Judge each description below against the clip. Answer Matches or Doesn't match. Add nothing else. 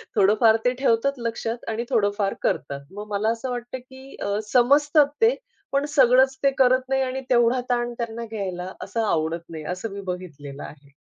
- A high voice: Matches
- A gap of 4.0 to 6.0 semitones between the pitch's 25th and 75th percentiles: Matches